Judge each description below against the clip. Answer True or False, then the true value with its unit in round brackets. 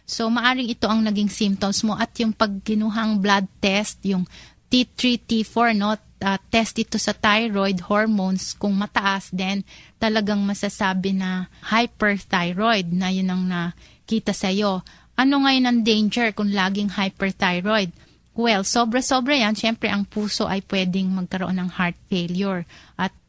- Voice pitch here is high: True (205 Hz)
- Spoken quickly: False (140 wpm)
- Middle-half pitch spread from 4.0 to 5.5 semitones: False (2.8 semitones)